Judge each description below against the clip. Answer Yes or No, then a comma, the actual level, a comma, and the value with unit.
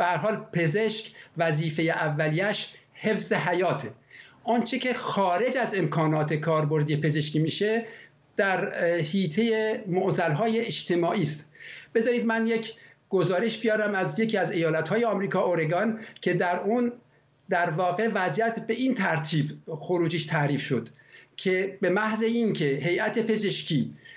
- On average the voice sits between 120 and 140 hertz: No, medium, 185 Hz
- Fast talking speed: No, average, 120 wpm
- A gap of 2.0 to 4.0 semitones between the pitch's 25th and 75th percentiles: No, wide, 5.4 semitones